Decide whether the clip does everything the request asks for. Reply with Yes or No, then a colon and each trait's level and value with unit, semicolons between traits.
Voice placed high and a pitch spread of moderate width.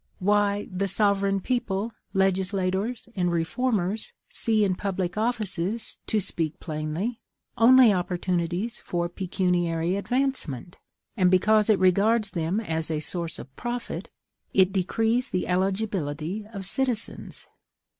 Yes: high, 195 Hz; average, 3.6 semitones